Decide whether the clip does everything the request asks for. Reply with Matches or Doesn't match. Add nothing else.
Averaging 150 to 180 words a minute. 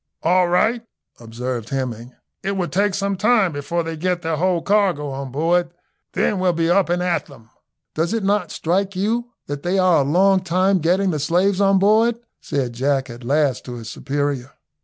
Doesn't match